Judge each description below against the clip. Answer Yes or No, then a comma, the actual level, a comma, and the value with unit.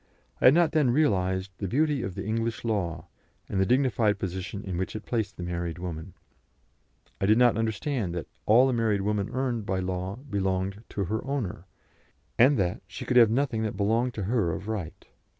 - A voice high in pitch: No, low, 105 Hz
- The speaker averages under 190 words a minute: No, average, 195 wpm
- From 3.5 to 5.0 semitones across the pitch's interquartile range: Yes, average, 4.4 semitones